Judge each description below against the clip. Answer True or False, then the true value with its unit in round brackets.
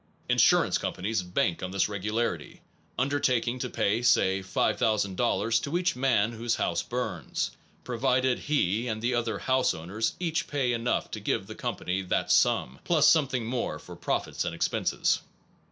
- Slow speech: False (165 wpm)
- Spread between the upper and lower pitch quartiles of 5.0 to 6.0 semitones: False (4.2 semitones)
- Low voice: True (115 Hz)